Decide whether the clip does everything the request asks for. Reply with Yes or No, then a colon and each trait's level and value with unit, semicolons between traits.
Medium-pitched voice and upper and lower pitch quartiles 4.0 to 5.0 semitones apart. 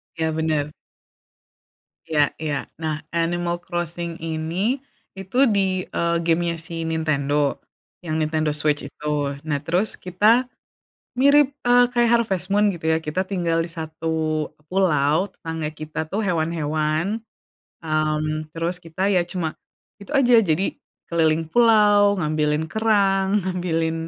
No: medium, 165 Hz; average, 3.6 semitones